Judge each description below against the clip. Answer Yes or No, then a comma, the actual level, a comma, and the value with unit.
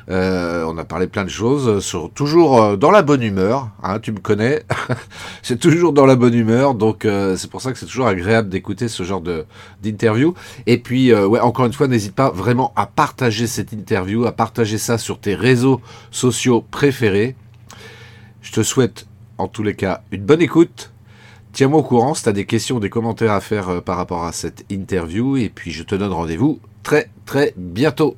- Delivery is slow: No, average, 205 wpm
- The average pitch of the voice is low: Yes, low, 110 Hz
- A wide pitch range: No, average, 4.0 semitones